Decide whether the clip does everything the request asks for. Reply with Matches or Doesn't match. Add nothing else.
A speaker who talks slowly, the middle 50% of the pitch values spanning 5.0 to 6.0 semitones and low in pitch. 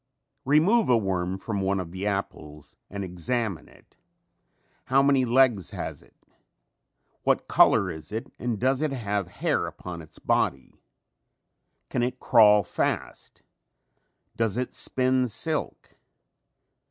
Matches